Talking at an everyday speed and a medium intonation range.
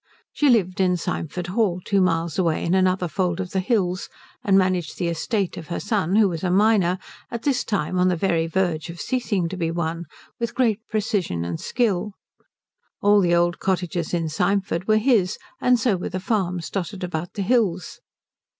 Yes: average, 190 wpm; average, 3.1 semitones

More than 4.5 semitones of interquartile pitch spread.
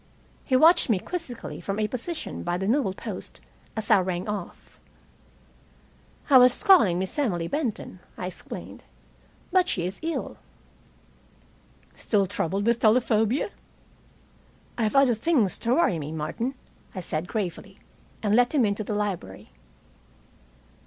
Yes: wide, 5.5 semitones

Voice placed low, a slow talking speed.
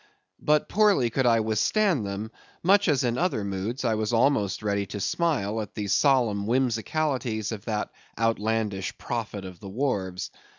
No: low, 115 Hz; average, 160 wpm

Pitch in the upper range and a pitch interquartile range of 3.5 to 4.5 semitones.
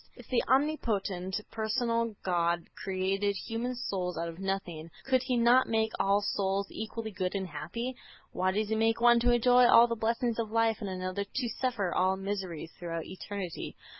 Yes: high, 205 Hz; average, 3.8 semitones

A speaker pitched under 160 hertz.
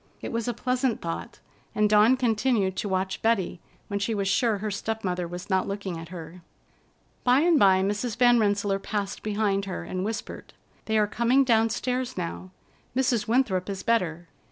No: high, 210 Hz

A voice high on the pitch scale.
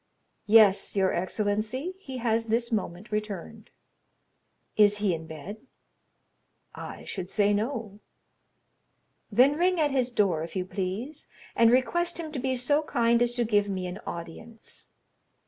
Yes: high, 220 Hz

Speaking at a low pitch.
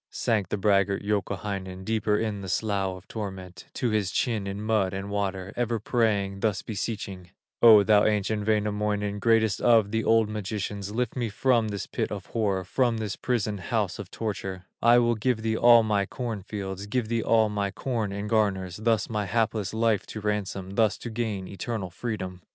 Yes: low, 105 Hz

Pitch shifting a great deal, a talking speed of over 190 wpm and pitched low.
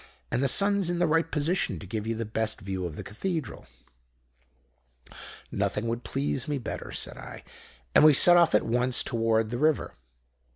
No: wide, 6.3 semitones; average, 180 wpm; low, 125 Hz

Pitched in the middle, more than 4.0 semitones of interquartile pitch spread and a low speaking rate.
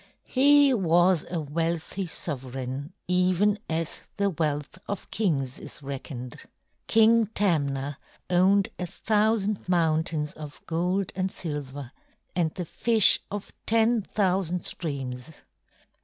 Yes: medium, 175 Hz; average, 5.3 semitones; slow, 110 wpm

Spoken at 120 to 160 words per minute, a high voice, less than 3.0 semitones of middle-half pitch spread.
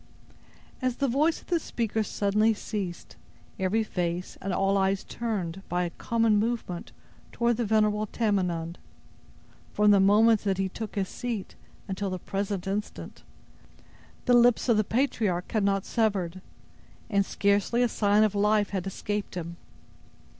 Yes: average, 150 wpm; high, 205 Hz; narrow, 2.6 semitones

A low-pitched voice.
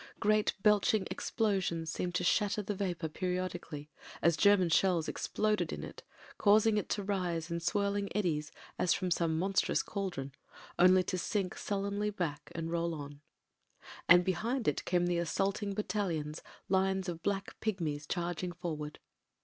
No: medium, 180 Hz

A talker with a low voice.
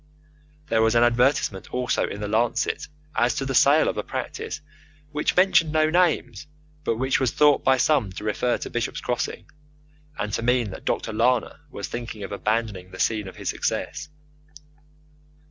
Yes: low, 120 Hz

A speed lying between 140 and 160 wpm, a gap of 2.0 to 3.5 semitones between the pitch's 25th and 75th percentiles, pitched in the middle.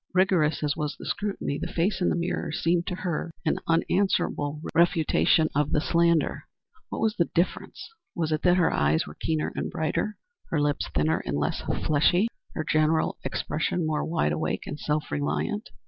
No: average, 180 wpm; average, 2.8 semitones; medium, 160 Hz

